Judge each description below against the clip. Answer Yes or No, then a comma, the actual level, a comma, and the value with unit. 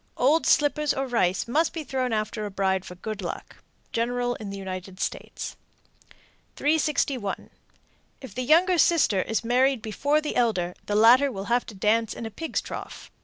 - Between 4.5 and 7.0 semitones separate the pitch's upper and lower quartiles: Yes, wide, 5.5 semitones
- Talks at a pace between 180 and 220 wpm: No, average, 170 wpm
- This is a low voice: No, high, 235 Hz